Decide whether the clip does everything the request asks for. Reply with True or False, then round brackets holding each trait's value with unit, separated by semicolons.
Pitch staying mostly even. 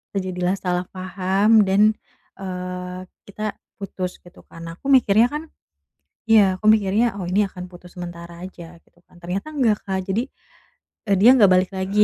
True (2.0 semitones)